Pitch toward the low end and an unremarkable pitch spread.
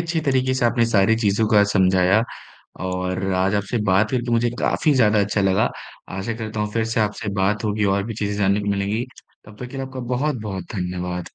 Yes: low, 105 Hz; average, 3.2 semitones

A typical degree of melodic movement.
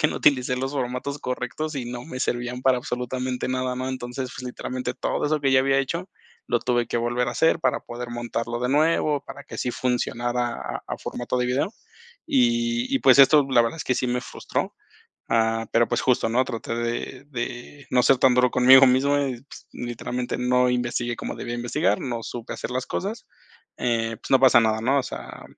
No: narrow, 1.9 semitones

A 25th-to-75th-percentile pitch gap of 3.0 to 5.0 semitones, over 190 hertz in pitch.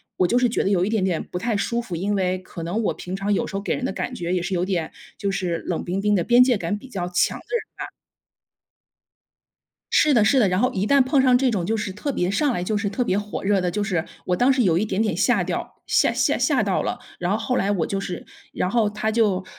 Yes: average, 4.2 semitones; high, 200 Hz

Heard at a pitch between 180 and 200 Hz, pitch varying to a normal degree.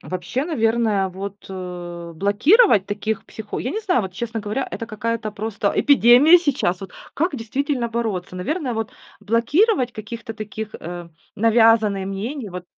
No: high, 220 Hz; average, 3.8 semitones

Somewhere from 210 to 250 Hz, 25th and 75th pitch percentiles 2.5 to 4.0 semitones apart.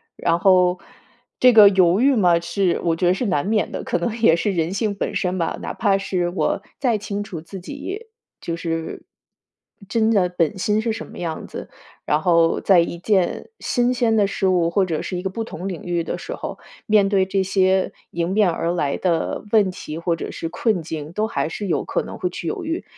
No: medium, 185 Hz; average, 3.6 semitones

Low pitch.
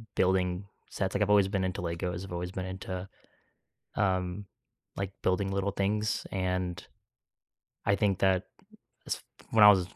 Yes: very low, 95 Hz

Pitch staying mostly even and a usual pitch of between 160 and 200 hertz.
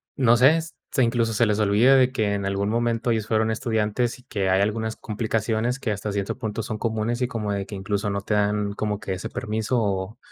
No: narrow, 2.3 semitones; low, 110 Hz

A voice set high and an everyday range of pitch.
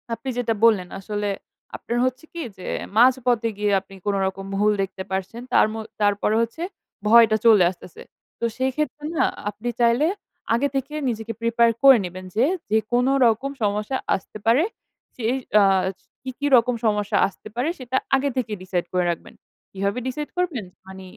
Yes: high, 225 Hz; average, 4.0 semitones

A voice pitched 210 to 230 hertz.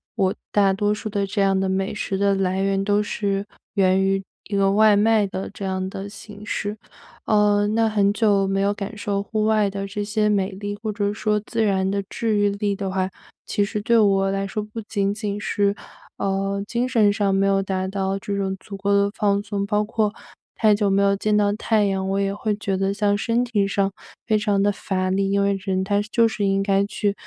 No: high, 200 Hz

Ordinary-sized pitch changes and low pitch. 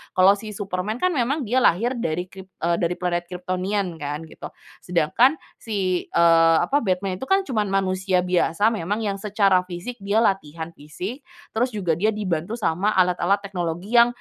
No: average, 3.6 semitones; high, 190 Hz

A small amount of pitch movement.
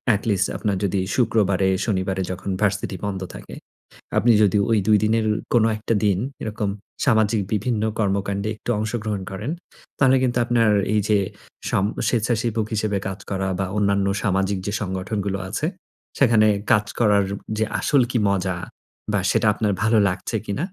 Yes: narrow, 2.3 semitones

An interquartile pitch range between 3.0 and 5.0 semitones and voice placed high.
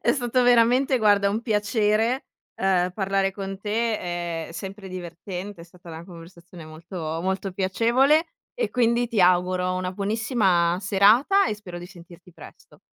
Yes: average, 4.0 semitones; high, 195 Hz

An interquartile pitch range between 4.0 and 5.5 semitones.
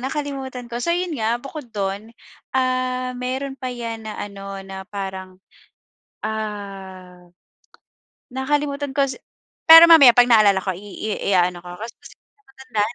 Yes: average, 5.0 semitones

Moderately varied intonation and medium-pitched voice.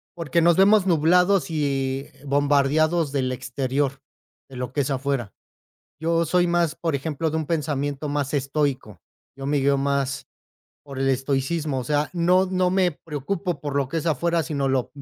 Yes: average, 3.5 semitones; medium, 145 Hz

